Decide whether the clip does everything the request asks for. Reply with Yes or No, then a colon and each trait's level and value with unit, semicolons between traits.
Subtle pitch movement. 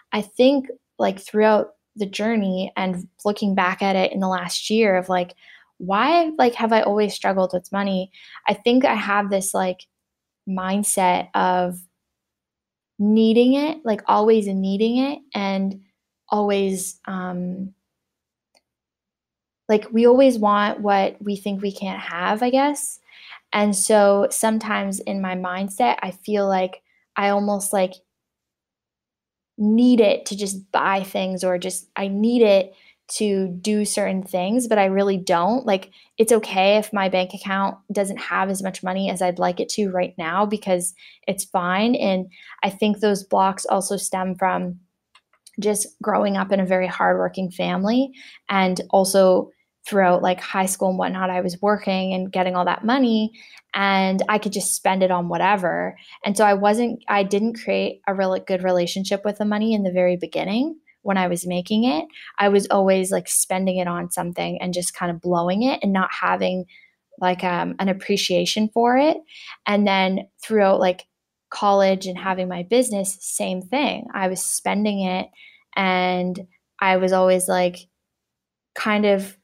Yes: narrow, 2.3 semitones